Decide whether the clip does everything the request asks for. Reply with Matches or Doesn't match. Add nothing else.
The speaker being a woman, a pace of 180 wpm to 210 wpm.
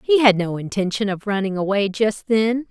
Matches